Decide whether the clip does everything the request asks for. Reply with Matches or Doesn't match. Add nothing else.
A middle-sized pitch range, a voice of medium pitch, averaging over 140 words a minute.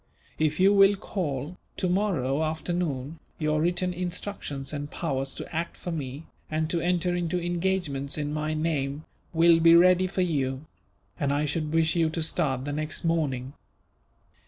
Matches